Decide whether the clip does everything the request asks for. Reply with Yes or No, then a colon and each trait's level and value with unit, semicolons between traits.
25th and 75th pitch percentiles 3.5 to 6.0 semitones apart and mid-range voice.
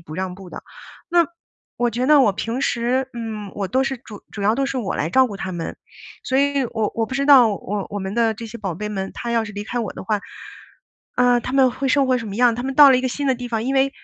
No: average, 4.1 semitones; high, 235 Hz